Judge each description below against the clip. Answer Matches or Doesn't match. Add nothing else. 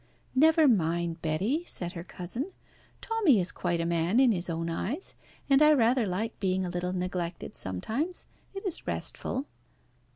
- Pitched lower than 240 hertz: Matches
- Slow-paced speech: Doesn't match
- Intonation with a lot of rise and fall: Matches